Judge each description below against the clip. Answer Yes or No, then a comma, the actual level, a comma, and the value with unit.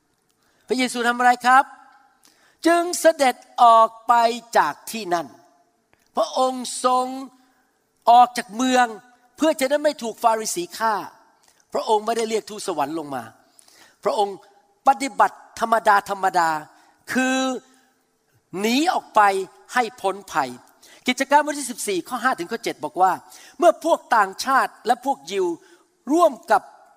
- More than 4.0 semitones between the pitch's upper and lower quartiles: Yes, average, 4.4 semitones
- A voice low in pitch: No, high, 245 Hz